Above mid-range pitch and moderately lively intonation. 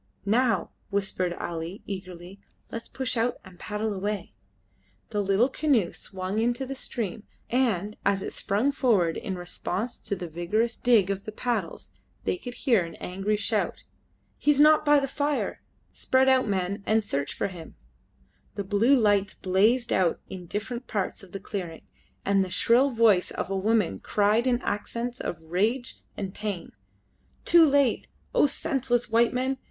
Yes: high, 210 Hz; average, 4.5 semitones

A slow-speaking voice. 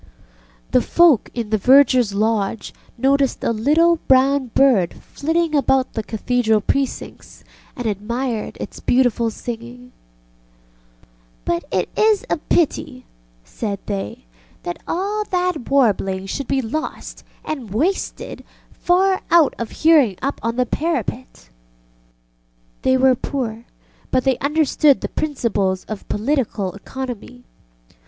Yes: slow, 120 wpm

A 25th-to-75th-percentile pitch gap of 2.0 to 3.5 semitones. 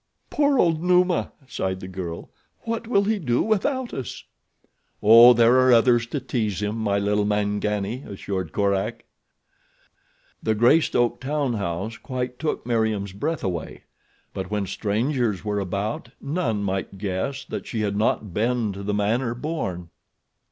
No: average, 4.3 semitones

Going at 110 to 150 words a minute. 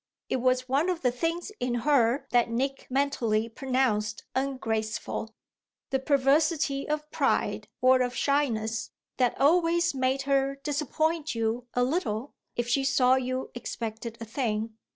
Yes: average, 140 wpm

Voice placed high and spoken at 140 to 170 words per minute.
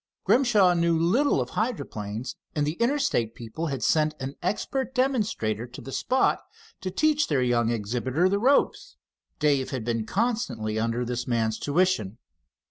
No: medium, 145 Hz; average, 150 wpm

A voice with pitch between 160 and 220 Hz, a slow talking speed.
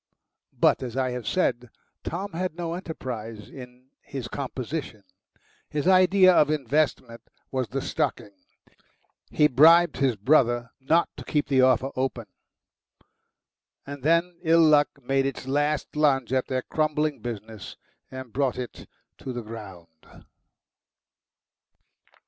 No: low, 135 Hz; slow, 125 wpm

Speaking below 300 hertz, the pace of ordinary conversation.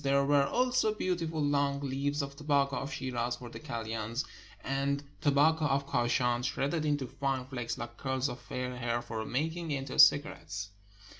Yes: medium, 140 Hz; average, 165 wpm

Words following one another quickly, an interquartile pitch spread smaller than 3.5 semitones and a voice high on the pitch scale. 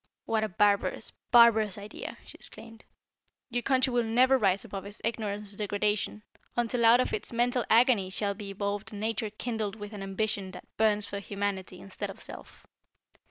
No: average, 175 wpm; narrow, 2.4 semitones; high, 210 Hz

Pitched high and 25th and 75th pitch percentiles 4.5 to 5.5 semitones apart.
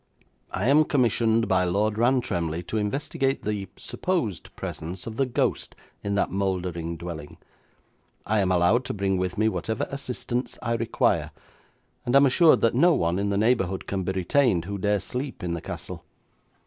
No: low, 105 Hz; average, 4.9 semitones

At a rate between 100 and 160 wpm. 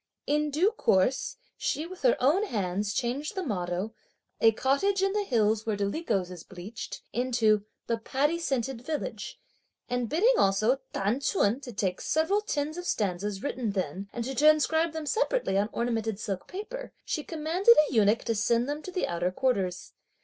No: average, 175 wpm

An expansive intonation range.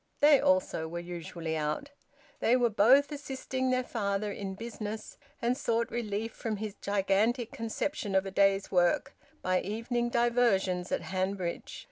No: average, 3.9 semitones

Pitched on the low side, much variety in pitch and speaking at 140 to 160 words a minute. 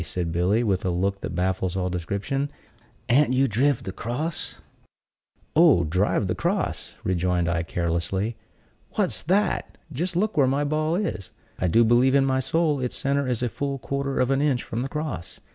No: low, 125 Hz; wide, 7.2 semitones; average, 180 wpm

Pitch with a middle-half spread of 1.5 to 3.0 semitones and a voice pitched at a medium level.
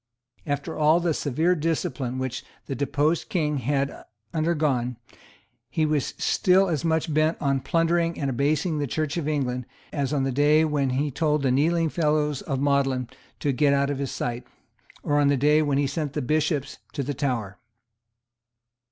Yes: narrow, 2.4 semitones; medium, 145 Hz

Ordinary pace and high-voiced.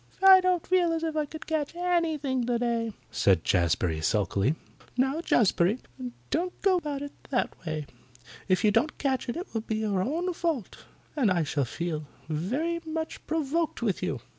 Yes: average, 170 wpm; very high, 265 Hz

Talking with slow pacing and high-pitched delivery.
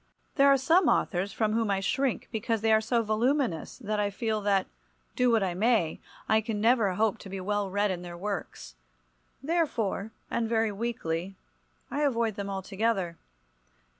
No: average, 170 wpm; high, 215 Hz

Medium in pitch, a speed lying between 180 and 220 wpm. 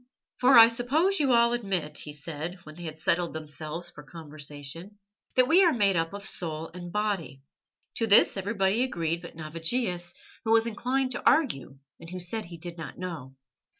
Yes: medium, 175 Hz; average, 185 wpm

